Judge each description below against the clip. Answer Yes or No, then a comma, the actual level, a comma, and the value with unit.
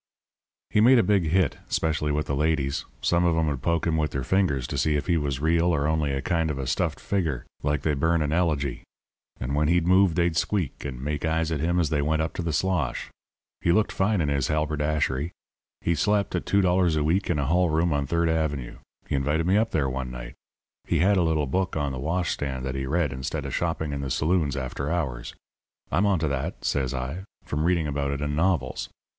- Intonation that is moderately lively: Yes, average, 3.4 semitones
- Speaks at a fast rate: Yes, fast, 230 wpm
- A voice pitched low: Yes, very low, 80 Hz